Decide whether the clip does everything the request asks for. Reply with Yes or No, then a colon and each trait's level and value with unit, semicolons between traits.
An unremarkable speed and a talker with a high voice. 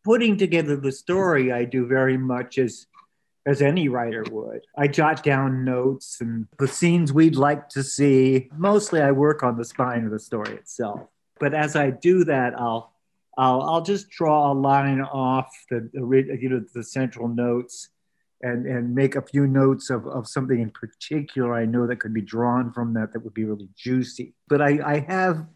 No: average, 190 wpm; low, 130 Hz